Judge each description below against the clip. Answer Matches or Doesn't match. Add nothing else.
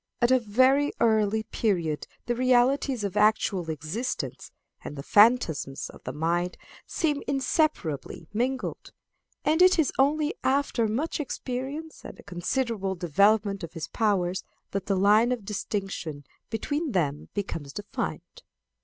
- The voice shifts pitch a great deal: Matches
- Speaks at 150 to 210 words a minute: Doesn't match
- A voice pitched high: Matches